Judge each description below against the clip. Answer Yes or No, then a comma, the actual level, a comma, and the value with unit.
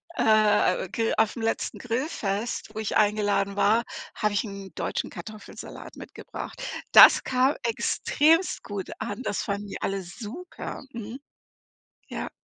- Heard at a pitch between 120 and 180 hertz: No, high, 215 Hz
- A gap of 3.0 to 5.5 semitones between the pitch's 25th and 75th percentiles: No, narrow, 2.6 semitones